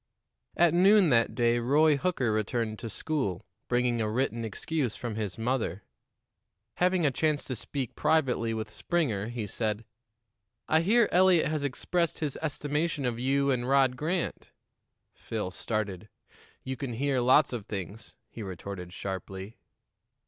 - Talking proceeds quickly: No, average, 145 wpm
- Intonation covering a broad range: Yes, wide, 5.7 semitones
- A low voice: Yes, low, 125 Hz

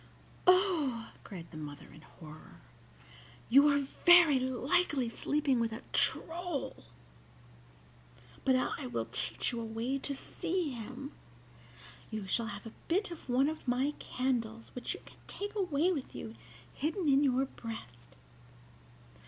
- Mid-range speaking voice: No, very high, 260 Hz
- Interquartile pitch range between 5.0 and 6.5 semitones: Yes, wide, 5.4 semitones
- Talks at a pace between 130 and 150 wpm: Yes, average, 140 wpm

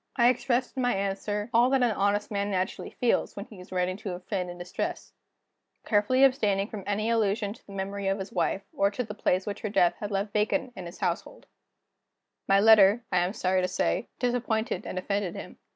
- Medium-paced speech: No, fast, 215 wpm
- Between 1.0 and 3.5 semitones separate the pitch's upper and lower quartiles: Yes, narrow, 2.6 semitones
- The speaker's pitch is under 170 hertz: No, high, 200 Hz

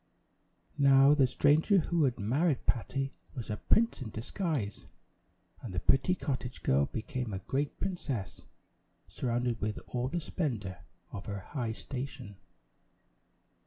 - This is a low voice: Yes, low, 130 Hz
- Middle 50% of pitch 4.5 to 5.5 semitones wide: Yes, average, 5.1 semitones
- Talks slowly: Yes, slow, 130 wpm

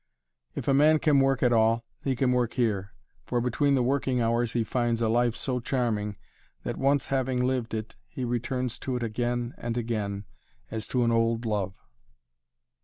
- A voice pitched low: Yes, low, 120 Hz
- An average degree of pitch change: No, narrow, 2.1 semitones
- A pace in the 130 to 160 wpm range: No, average, 180 wpm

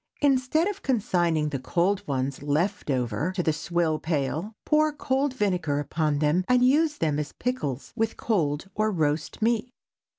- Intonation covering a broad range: Yes, wide, 8.6 semitones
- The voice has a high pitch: No, medium, 175 Hz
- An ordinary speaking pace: Yes, average, 155 wpm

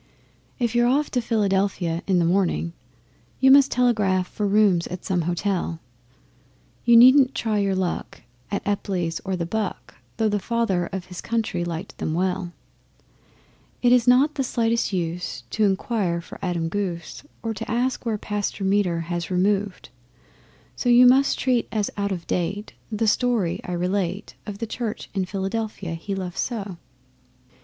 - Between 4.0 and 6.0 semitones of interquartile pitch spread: Yes, average, 4.3 semitones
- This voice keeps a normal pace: Yes, average, 160 wpm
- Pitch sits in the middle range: No, high, 200 Hz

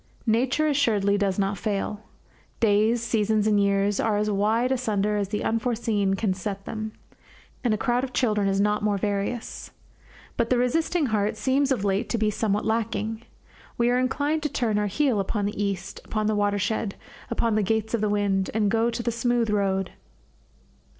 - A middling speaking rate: Yes, average, 185 wpm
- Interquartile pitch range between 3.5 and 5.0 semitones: No, narrow, 2.6 semitones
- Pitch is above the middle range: Yes, high, 215 Hz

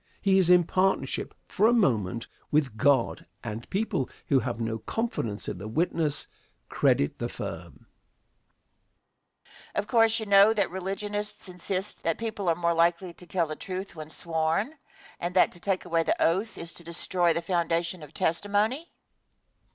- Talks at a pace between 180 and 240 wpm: No, average, 165 wpm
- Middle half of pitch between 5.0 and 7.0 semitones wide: No, average, 3.9 semitones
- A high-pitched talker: No, medium, 175 Hz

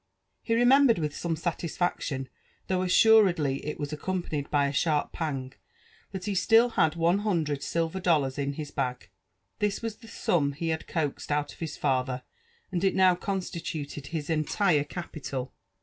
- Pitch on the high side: No, medium, 160 Hz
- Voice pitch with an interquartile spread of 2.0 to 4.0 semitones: No, average, 4.5 semitones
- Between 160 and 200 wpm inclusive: Yes, average, 165 wpm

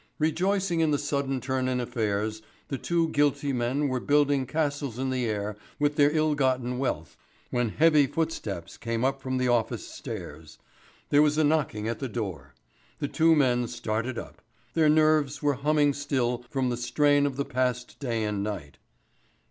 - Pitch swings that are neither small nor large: Yes, average, 3.6 semitones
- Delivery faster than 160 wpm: Yes, average, 175 wpm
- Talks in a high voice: No, low, 135 Hz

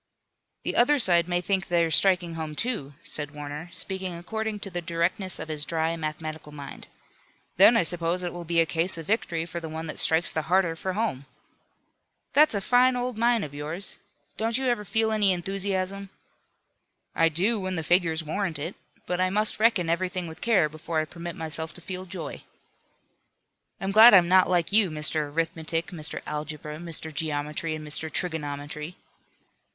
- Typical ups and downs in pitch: Yes, average, 3.4 semitones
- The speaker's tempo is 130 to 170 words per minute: No, average, 180 wpm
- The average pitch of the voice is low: No, medium, 170 Hz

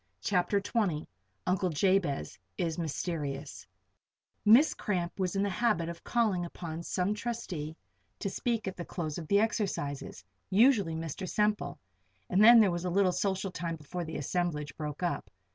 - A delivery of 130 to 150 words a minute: No, average, 160 wpm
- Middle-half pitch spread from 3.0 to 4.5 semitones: Yes, average, 3.8 semitones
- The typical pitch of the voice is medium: Yes, medium, 180 Hz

